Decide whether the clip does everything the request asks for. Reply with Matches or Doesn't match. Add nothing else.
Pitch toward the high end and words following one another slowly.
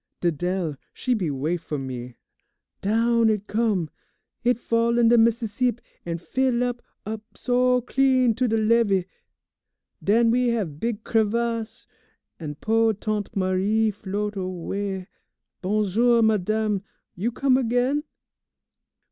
Matches